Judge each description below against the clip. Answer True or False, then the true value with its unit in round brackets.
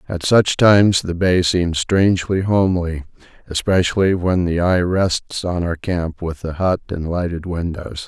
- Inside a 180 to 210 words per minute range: False (165 wpm)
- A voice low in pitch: True (90 Hz)